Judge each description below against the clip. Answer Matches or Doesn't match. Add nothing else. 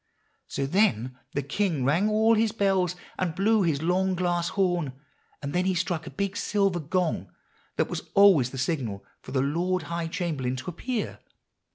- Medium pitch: Matches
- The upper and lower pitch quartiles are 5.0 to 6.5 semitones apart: Matches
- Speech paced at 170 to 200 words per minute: Matches